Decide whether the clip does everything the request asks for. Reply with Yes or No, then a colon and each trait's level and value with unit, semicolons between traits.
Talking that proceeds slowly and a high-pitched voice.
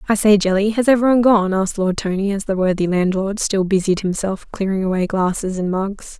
No: fast, 205 wpm; high, 195 Hz